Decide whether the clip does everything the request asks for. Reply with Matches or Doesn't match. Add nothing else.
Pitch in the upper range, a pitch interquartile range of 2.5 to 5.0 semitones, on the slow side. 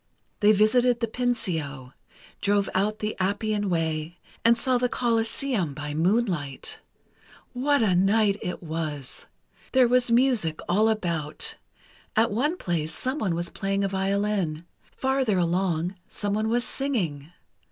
Doesn't match